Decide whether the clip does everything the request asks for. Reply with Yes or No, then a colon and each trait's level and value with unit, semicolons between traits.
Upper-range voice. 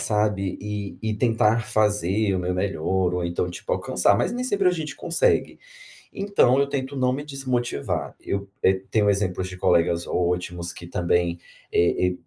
No: low, 100 Hz